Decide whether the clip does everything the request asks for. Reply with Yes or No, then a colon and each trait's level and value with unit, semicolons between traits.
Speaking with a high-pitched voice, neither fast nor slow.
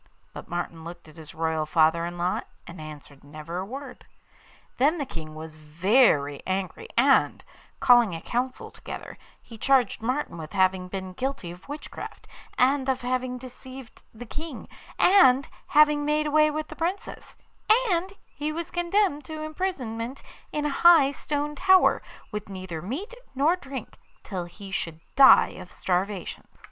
Yes: high, 245 Hz; average, 155 wpm